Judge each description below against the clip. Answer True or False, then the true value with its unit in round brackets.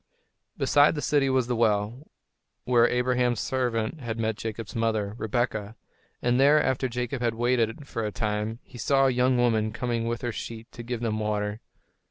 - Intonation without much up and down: True (2.2 semitones)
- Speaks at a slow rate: False (180 wpm)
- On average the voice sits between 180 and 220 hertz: False (120 Hz)